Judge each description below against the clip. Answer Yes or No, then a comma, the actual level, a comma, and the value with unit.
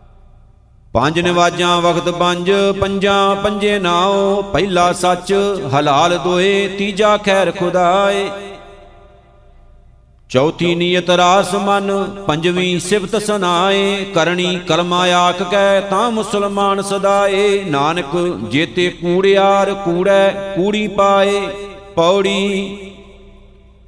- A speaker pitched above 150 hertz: Yes, high, 190 Hz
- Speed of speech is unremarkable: No, slow, 90 wpm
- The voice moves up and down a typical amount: No, narrow, 2.3 semitones